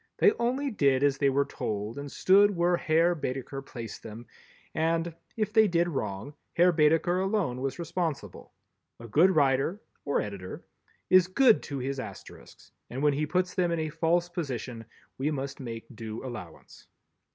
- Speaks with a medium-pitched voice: Yes, medium, 150 Hz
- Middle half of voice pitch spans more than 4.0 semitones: Yes, average, 5.3 semitones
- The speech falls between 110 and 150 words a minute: No, average, 160 wpm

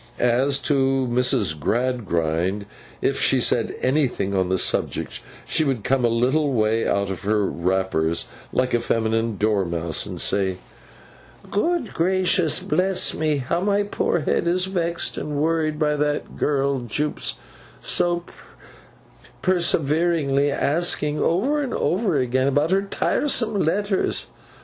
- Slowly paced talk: Yes, slow, 130 wpm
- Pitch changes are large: Yes, wide, 7.4 semitones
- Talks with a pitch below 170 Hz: Yes, medium, 140 Hz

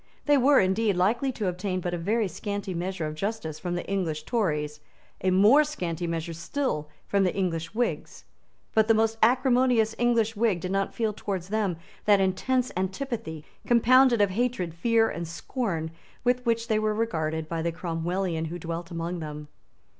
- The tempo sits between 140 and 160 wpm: No, average, 175 wpm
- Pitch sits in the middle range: No, high, 195 Hz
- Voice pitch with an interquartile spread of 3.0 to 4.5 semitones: No, average, 5.3 semitones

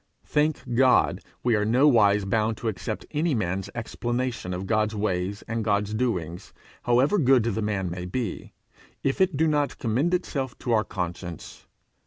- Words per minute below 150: No, average, 160 wpm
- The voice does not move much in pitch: No, average, 4.3 semitones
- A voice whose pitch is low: Yes, low, 115 Hz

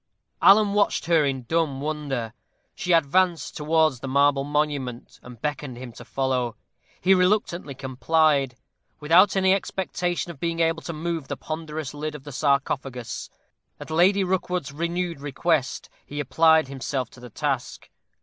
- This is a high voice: No, medium, 150 Hz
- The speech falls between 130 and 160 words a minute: Yes, average, 150 wpm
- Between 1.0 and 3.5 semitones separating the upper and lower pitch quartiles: No, average, 3.9 semitones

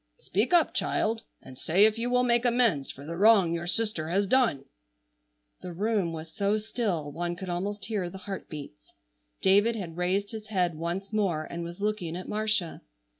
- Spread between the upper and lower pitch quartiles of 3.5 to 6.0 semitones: Yes, average, 4.2 semitones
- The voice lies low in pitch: No, high, 195 Hz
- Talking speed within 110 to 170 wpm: No, average, 180 wpm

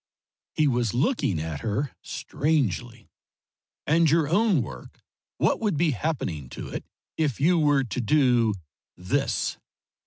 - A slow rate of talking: Yes, slow, 130 wpm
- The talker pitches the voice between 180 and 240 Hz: No, low, 135 Hz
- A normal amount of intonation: No, wide, 6.4 semitones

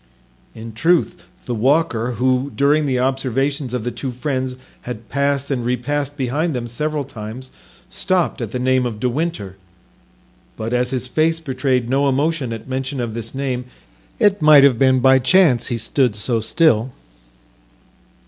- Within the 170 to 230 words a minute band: No, average, 160 wpm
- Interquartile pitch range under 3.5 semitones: Yes, average, 2.9 semitones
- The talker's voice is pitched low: Yes, low, 130 Hz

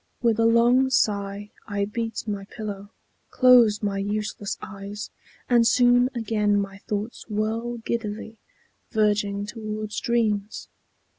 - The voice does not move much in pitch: Yes, narrow, 2.2 semitones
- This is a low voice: No, high, 215 Hz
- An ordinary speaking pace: No, slow, 120 wpm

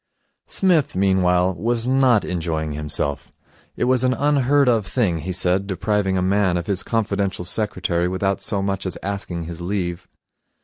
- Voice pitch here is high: No, very low, 95 Hz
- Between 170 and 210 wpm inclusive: No, average, 160 wpm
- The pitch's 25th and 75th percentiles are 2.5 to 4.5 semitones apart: Yes, average, 4.0 semitones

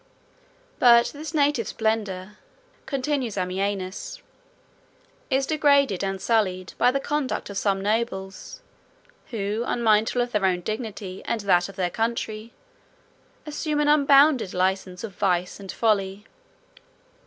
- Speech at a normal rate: No, slow, 125 wpm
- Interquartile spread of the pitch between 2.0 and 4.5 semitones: No, wide, 5.4 semitones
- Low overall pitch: No, high, 215 Hz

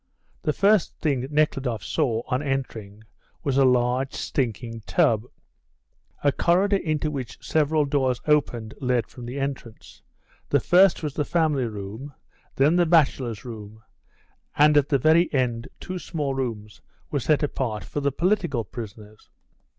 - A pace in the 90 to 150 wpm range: Yes, average, 145 wpm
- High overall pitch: No, low, 135 Hz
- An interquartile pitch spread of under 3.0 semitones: No, average, 4.5 semitones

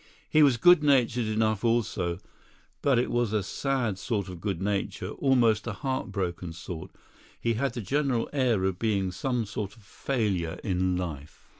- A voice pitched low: Yes, low, 110 Hz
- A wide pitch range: No, average, 4.7 semitones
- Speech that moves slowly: No, average, 170 wpm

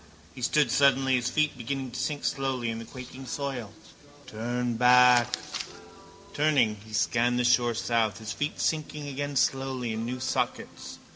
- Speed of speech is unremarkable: Yes, average, 155 wpm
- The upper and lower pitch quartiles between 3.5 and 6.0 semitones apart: No, narrow, 2.5 semitones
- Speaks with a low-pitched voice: Yes, low, 125 Hz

